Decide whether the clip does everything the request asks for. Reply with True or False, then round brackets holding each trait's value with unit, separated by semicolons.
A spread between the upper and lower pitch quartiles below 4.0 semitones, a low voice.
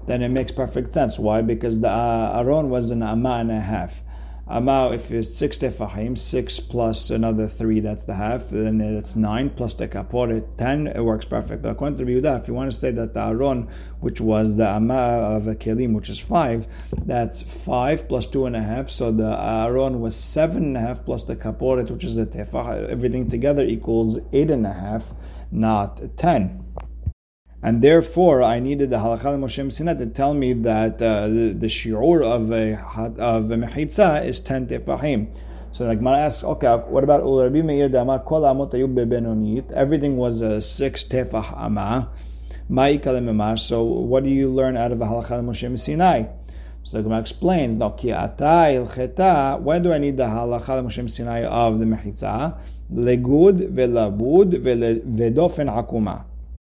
True (3.2 semitones; 115 Hz)